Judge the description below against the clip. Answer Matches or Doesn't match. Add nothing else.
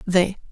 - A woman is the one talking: Matches